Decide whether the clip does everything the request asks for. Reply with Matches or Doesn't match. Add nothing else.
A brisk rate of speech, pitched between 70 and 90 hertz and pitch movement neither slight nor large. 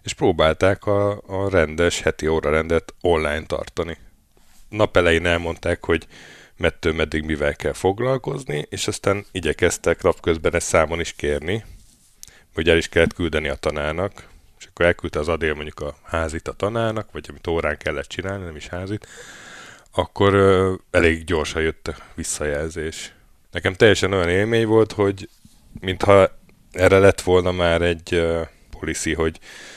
Doesn't match